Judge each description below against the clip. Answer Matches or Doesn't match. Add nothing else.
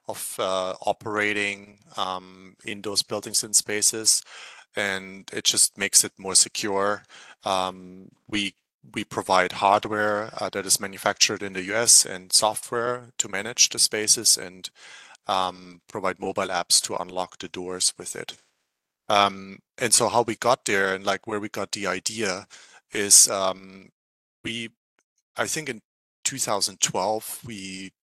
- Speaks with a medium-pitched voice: Doesn't match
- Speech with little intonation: Matches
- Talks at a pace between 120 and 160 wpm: Matches